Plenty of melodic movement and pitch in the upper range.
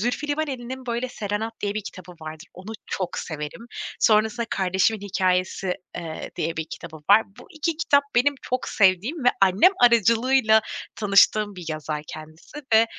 No: average, 5.0 semitones; high, 210 Hz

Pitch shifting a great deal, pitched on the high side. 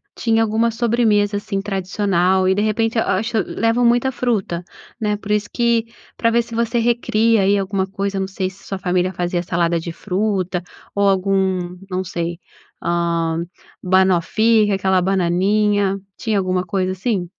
No: average, 3.2 semitones; high, 195 Hz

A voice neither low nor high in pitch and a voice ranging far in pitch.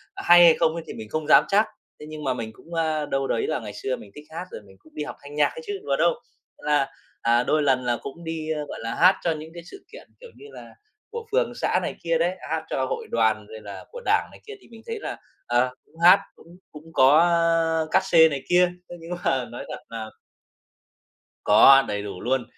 No: medium, 155 Hz; average, 4.9 semitones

